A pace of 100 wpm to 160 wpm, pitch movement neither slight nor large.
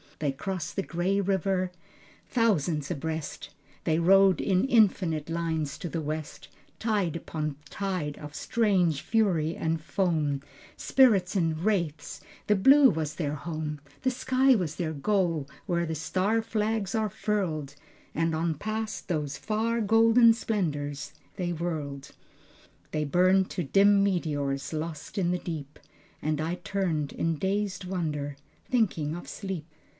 Yes: average, 140 wpm; average, 4.6 semitones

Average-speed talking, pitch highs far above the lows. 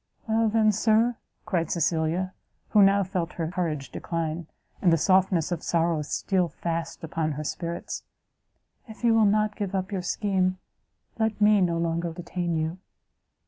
No: average, 155 wpm; average, 3.6 semitones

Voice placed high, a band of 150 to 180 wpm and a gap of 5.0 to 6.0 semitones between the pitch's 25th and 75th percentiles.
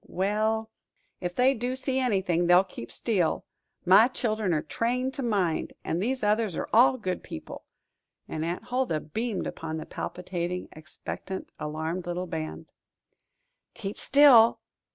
No: high, 195 Hz; average, 140 wpm; average, 5.3 semitones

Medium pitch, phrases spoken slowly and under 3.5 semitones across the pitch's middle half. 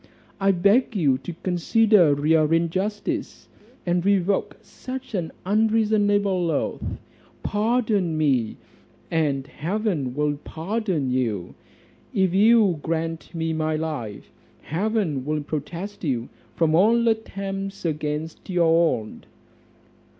No: medium, 170 Hz; slow, 105 wpm; average, 5.0 semitones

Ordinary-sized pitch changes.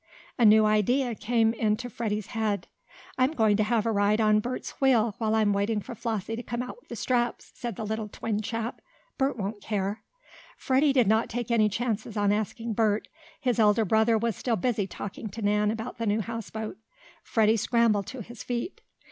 No: narrow, 2.0 semitones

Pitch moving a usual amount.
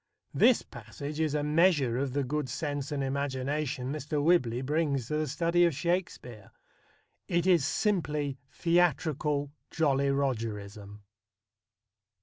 Yes: average, 3.1 semitones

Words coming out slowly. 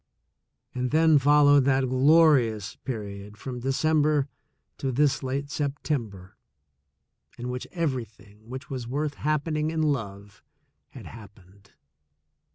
Yes: slow, 115 wpm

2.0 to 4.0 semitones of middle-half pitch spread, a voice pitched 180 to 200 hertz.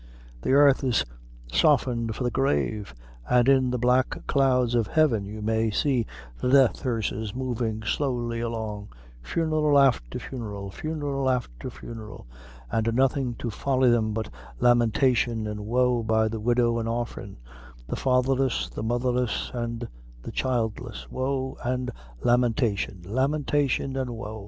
No: average, 2.8 semitones; low, 120 Hz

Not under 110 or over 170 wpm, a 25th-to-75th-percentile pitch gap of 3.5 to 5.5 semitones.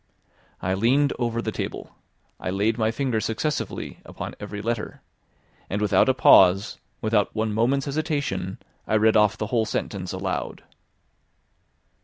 No: average, 140 wpm; average, 3.1 semitones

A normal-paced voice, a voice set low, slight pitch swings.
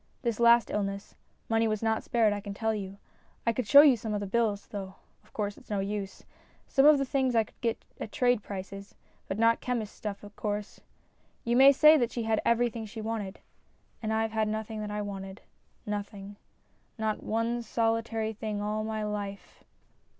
No: average, 190 wpm; high, 220 Hz; narrow, 2.0 semitones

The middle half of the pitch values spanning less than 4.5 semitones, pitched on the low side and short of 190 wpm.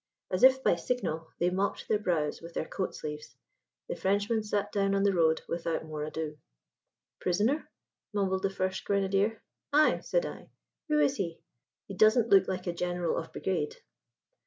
No: average, 3.6 semitones; high, 190 Hz; average, 170 wpm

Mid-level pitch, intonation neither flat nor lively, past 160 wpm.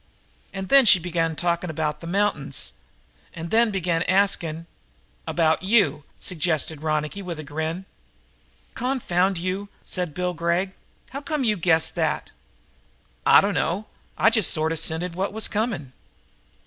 No: medium, 175 Hz; average, 3.8 semitones; average, 145 wpm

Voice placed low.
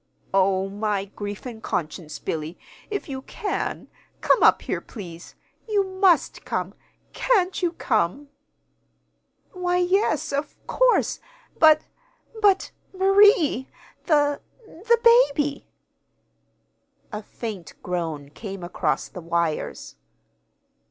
No: very high, 280 Hz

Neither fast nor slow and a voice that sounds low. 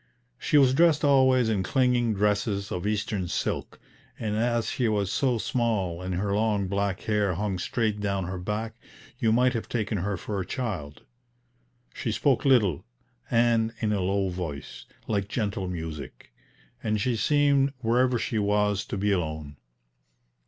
Yes: average, 160 wpm; low, 105 Hz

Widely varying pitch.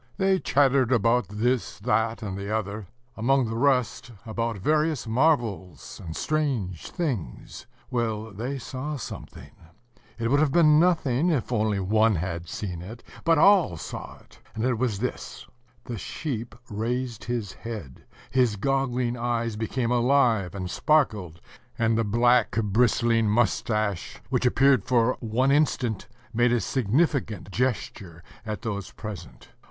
No: average, 3.6 semitones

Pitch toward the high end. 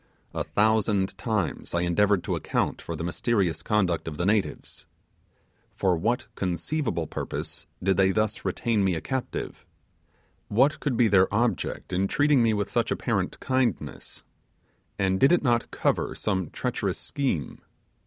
No: low, 105 Hz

